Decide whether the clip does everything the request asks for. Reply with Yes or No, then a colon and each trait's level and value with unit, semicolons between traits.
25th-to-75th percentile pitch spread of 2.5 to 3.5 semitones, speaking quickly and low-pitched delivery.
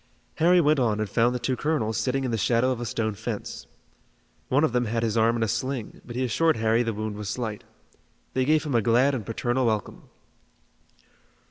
Yes: average, 2.8 semitones; fast, 215 wpm; low, 120 Hz